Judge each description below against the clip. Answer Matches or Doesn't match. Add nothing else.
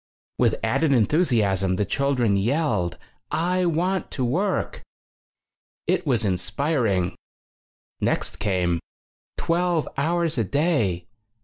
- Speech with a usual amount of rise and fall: Doesn't match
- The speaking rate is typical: Doesn't match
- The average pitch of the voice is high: Doesn't match